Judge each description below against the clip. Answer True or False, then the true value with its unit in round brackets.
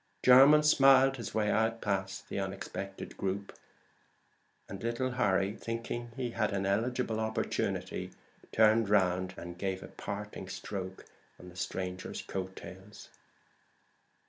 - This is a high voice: False (100 Hz)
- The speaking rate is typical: False (125 wpm)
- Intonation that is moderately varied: True (3.4 semitones)